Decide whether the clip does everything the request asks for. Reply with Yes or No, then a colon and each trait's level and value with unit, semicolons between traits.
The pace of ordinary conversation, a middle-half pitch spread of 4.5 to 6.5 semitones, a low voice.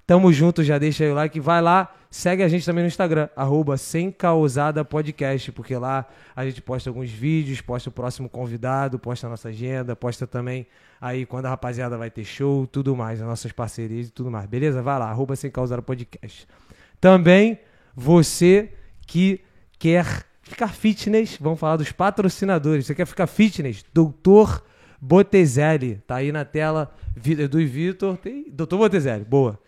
No: average, 160 wpm; wide, 5.5 semitones; medium, 145 Hz